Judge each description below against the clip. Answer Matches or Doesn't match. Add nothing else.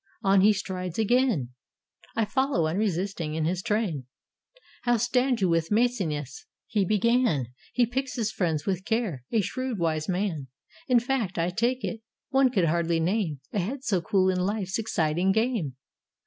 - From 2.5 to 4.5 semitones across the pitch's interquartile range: Doesn't match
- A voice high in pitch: Matches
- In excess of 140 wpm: Matches